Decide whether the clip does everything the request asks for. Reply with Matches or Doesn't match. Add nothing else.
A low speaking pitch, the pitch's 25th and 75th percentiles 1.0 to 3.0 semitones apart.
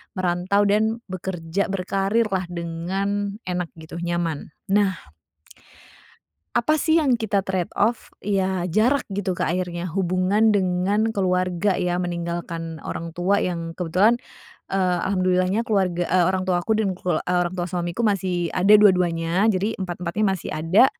Doesn't match